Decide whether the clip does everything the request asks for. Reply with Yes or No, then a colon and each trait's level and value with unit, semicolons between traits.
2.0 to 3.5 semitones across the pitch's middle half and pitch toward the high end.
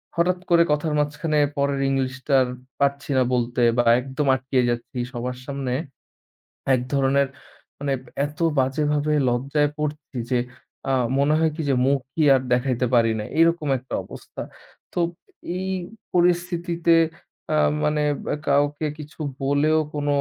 No: narrow, 2.6 semitones; medium, 140 Hz